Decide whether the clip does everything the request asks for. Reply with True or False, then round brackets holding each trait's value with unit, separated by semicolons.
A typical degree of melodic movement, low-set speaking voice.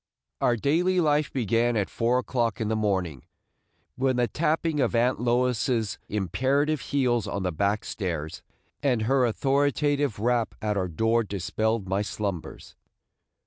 True (4.5 semitones; 115 Hz)